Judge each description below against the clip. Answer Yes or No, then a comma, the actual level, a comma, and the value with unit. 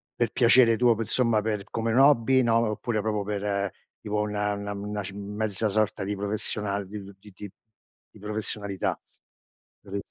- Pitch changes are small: Yes, narrow, 1.8 semitones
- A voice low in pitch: Yes, low, 105 Hz